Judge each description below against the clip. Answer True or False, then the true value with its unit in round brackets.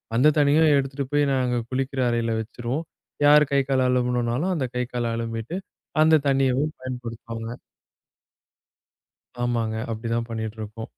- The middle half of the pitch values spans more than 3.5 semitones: False (3.1 semitones)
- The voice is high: False (125 Hz)